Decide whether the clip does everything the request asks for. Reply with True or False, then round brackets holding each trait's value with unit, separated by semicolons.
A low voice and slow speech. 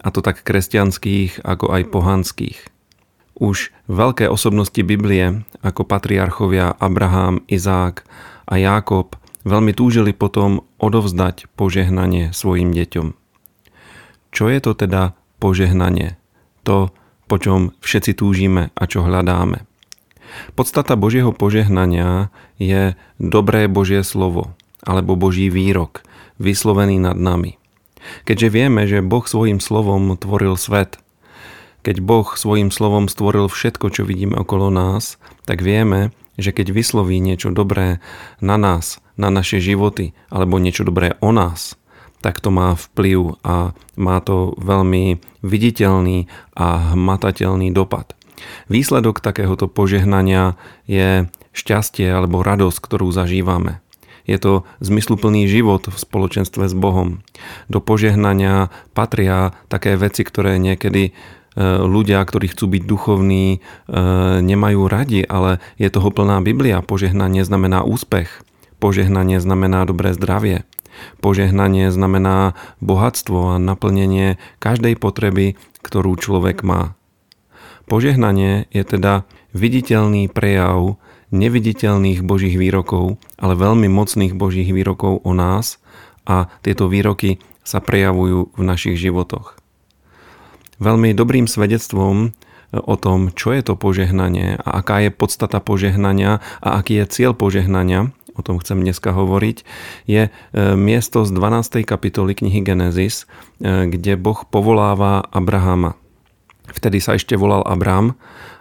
False (95 Hz; 120 wpm)